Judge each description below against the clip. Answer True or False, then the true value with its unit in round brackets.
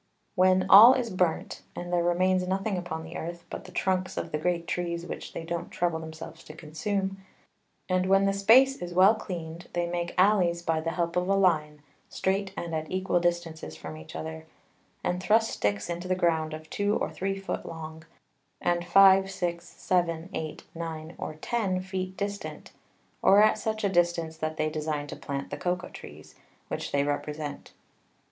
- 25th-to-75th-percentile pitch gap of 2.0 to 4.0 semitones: True (2.9 semitones)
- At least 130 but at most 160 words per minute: False (185 wpm)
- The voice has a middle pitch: True (175 Hz)